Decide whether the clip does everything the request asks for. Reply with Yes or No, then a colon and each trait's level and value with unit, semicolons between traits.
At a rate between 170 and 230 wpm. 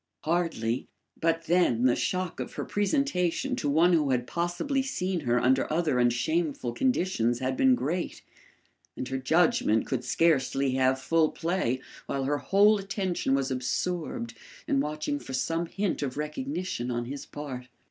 No: average, 155 wpm